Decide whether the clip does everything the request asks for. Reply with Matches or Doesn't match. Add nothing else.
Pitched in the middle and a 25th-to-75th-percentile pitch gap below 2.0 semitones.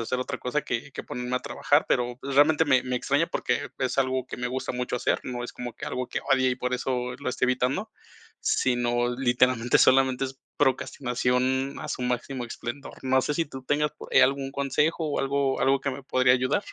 Doesn't match